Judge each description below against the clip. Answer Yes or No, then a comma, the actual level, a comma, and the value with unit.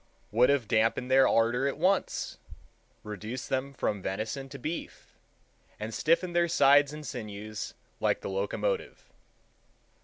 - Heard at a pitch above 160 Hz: No, low, 130 Hz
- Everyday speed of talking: No, slow, 130 wpm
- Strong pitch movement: No, average, 5.0 semitones